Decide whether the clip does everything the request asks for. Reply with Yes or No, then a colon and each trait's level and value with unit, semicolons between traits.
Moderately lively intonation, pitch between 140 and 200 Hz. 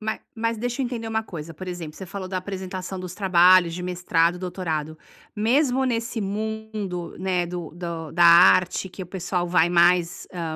Yes: average, 3.5 semitones; medium, 185 Hz